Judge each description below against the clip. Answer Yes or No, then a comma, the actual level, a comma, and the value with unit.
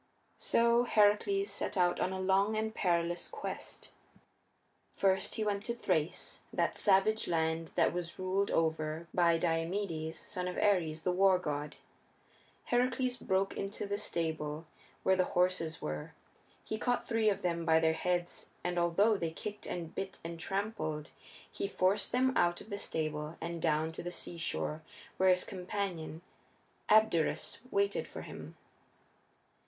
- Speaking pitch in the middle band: Yes, medium, 180 Hz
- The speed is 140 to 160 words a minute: Yes, average, 150 wpm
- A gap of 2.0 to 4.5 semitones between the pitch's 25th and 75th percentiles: Yes, average, 3.6 semitones